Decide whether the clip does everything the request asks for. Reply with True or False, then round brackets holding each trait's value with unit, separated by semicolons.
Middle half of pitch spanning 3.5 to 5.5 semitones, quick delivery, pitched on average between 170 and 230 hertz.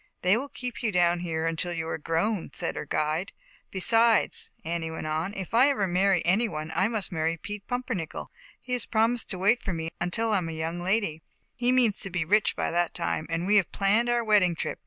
True (5.1 semitones; 240 wpm; 185 Hz)